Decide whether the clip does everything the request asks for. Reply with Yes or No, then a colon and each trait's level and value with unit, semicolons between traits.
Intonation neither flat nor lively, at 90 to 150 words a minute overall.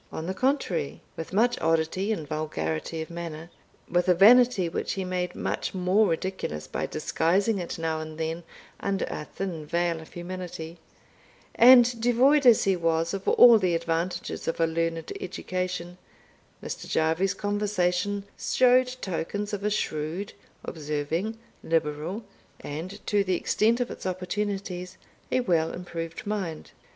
Yes: average, 3.9 semitones; average, 145 wpm